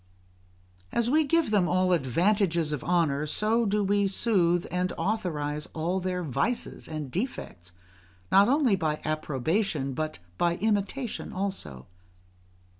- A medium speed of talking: No, slow, 125 wpm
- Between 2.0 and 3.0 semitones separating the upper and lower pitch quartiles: No, average, 5.1 semitones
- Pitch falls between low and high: Yes, medium, 180 Hz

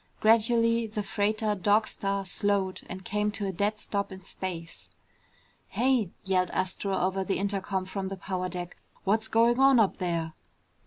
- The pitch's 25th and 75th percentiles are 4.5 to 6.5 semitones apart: No, narrow, 2.4 semitones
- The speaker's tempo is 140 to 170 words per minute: Yes, average, 160 wpm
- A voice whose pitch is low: No, high, 200 Hz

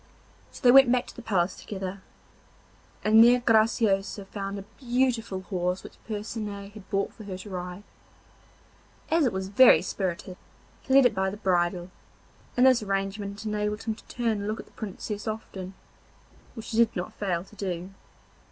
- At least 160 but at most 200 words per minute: Yes, average, 175 wpm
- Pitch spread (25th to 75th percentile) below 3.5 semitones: Yes, average, 2.9 semitones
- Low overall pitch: No, high, 205 Hz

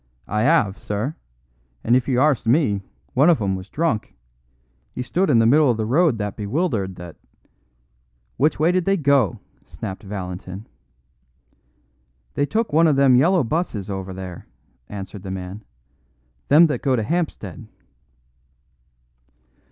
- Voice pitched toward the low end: Yes, low, 115 Hz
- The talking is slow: No, average, 150 wpm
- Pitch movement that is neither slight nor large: No, wide, 7.8 semitones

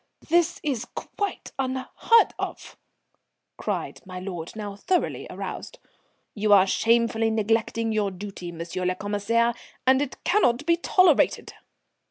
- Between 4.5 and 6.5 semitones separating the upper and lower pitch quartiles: Yes, average, 5.1 semitones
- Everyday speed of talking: No, slow, 125 wpm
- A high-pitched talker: Yes, high, 225 Hz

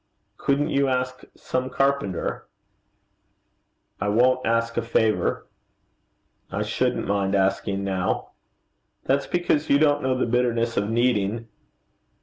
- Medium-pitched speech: No, low, 120 Hz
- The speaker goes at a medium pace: No, slow, 120 wpm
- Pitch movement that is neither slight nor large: Yes, average, 4.3 semitones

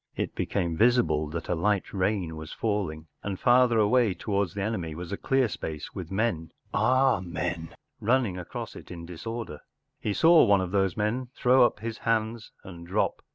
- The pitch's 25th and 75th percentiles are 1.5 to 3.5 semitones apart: No, average, 5.1 semitones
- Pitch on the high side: No, low, 100 Hz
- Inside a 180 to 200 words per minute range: Yes, average, 185 wpm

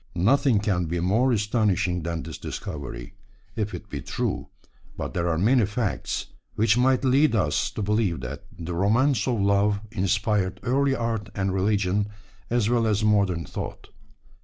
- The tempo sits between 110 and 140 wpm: No, average, 160 wpm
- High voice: No, low, 105 Hz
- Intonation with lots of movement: No, average, 4.3 semitones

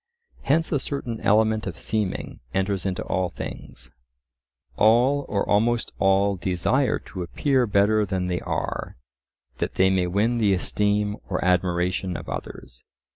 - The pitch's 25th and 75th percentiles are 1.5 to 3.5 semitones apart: Yes, average, 3.2 semitones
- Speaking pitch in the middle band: No, low, 100 Hz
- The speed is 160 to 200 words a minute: No, average, 140 wpm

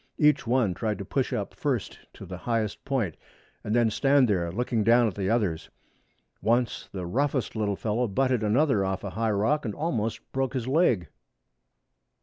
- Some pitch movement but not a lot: Yes, average, 4.2 semitones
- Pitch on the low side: Yes, low, 115 Hz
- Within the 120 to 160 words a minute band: No, average, 175 wpm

